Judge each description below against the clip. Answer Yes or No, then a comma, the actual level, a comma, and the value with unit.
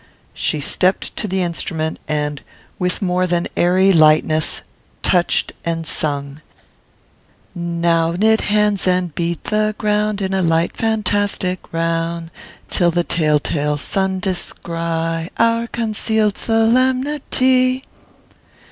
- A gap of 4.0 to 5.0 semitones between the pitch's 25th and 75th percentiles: Yes, average, 4.3 semitones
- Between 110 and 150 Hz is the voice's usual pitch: No, medium, 180 Hz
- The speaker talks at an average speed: No, slow, 110 wpm